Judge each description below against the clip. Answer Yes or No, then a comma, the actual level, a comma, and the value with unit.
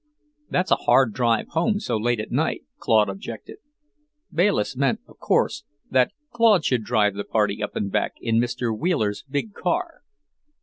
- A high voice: No, low, 120 Hz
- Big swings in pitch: Yes, wide, 7.9 semitones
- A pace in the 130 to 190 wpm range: Yes, average, 165 wpm